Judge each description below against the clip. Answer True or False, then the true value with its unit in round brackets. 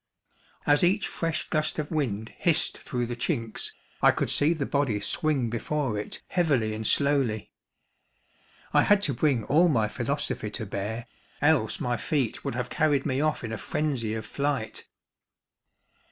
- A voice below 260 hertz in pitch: True (135 Hz)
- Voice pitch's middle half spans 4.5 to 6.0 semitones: True (5.2 semitones)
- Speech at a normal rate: True (160 wpm)